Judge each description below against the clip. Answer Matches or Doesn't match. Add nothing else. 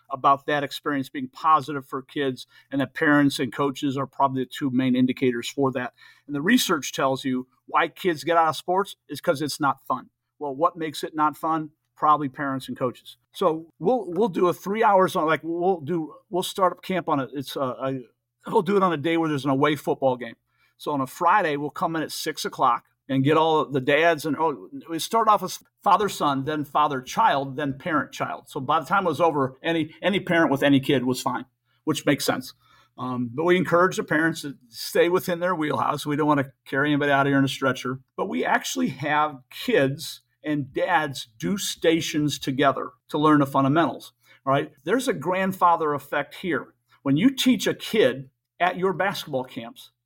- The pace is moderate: Doesn't match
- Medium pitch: Matches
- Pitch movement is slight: Doesn't match